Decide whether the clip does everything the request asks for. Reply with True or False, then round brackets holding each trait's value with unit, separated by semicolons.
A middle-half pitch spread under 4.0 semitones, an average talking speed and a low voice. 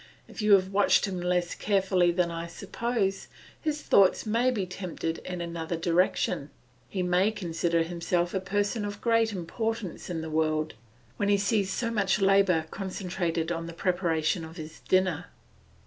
False (3.1 semitones; 165 wpm; 185 Hz)